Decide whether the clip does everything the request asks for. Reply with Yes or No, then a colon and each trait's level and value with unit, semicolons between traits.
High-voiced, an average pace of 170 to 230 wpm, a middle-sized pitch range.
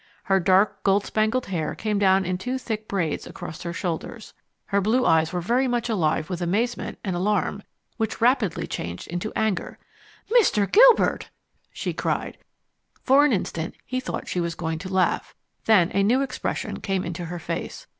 Yes: high, 195 Hz; average, 175 wpm; average, 4.4 semitones